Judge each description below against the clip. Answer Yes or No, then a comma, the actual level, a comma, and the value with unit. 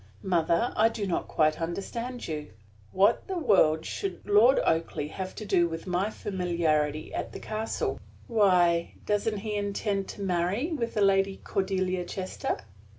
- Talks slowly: No, average, 150 wpm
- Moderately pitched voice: No, high, 195 Hz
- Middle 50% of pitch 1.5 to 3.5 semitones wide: No, average, 3.9 semitones